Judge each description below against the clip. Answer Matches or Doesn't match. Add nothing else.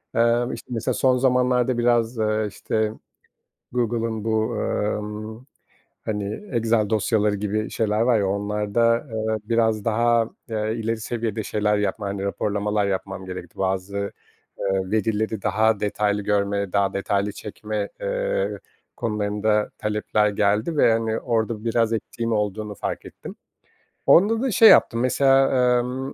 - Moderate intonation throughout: Doesn't match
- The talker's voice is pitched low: Matches